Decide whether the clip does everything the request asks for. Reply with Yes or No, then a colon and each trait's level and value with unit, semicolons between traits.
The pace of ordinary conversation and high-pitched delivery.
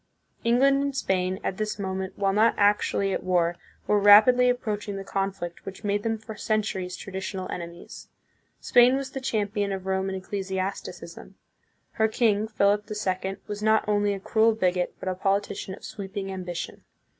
Yes: average, 165 wpm; high, 200 Hz